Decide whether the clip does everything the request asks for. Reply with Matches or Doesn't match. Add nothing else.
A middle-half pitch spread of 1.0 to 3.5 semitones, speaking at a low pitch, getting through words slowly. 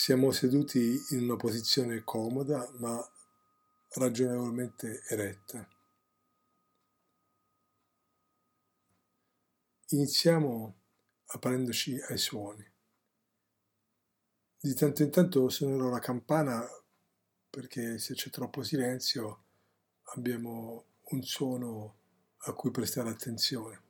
Matches